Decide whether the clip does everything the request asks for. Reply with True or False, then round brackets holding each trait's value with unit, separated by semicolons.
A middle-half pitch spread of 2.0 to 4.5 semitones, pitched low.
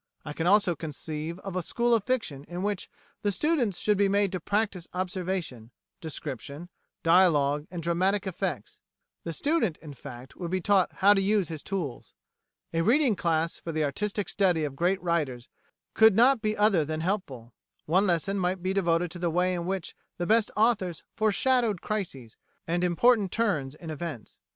False (4.1 semitones; 180 Hz)